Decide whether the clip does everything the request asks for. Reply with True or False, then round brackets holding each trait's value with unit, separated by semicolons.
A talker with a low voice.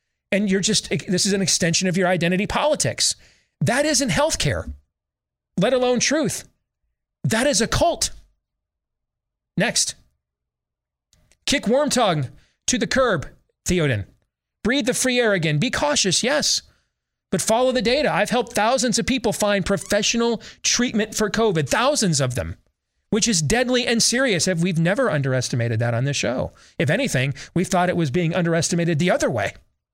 False (185 Hz)